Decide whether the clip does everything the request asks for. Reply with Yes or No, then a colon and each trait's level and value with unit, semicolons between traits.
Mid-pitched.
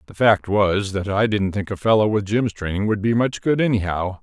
No: low, 105 Hz